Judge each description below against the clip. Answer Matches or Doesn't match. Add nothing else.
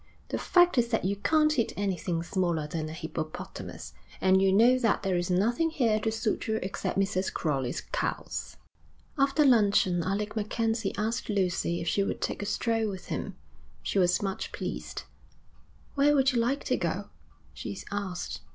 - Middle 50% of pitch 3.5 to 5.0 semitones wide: Matches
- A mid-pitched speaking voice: Doesn't match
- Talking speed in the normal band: Matches